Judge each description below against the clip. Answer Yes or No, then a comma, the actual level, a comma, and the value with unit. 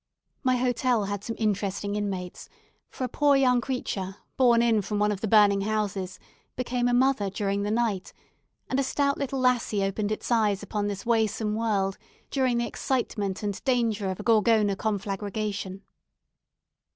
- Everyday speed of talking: Yes, average, 165 wpm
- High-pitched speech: Yes, high, 215 Hz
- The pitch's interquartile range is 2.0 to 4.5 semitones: Yes, average, 3.3 semitones